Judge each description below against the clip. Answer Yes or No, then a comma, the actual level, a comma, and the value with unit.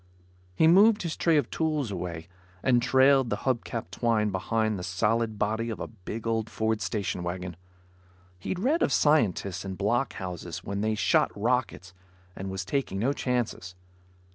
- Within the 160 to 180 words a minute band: Yes, average, 165 wpm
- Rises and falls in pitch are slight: No, average, 5.2 semitones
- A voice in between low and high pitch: No, low, 110 Hz